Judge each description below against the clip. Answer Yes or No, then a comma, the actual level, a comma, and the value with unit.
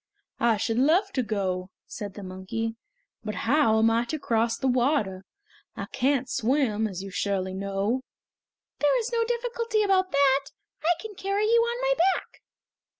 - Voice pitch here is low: No, very high, 250 Hz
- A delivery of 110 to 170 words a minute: Yes, average, 165 wpm